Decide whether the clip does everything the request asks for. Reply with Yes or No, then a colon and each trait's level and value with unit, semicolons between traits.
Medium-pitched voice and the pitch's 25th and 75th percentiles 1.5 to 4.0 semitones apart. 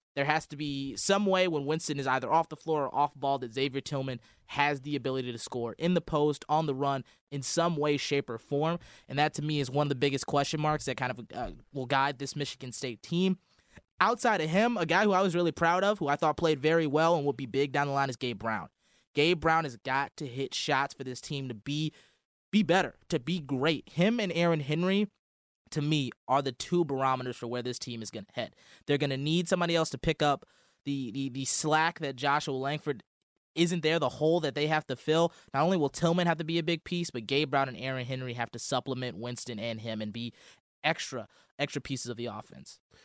Yes: medium, 145 Hz; average, 3.6 semitones